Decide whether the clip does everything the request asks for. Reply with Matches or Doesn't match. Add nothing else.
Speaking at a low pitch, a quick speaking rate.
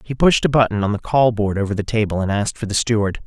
Matches